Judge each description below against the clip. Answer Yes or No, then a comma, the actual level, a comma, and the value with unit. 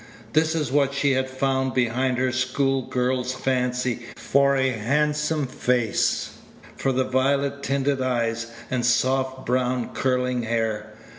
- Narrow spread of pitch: Yes, narrow, 1.6 semitones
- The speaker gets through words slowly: Yes, slow, 130 wpm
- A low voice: Yes, low, 130 Hz